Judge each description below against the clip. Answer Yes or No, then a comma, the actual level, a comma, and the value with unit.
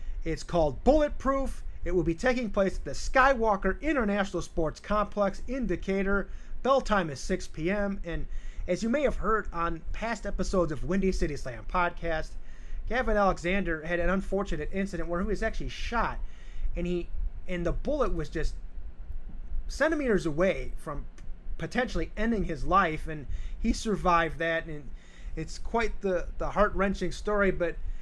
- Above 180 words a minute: No, average, 155 wpm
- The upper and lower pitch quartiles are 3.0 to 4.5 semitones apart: Yes, average, 4.0 semitones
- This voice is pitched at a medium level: Yes, medium, 180 Hz